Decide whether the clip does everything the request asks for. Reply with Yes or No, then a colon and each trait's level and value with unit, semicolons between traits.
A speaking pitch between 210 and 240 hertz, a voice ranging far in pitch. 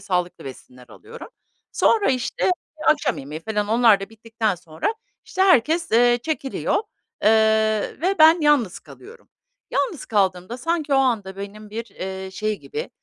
Yes: high, 225 Hz; wide, 7.5 semitones